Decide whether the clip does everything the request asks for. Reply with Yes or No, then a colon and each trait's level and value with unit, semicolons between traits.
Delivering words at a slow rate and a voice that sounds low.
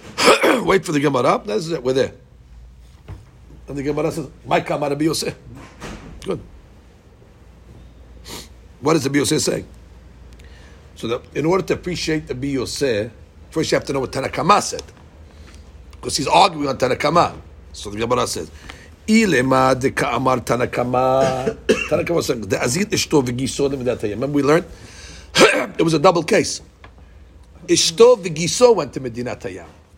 Yes: slow, 120 wpm; low, 120 Hz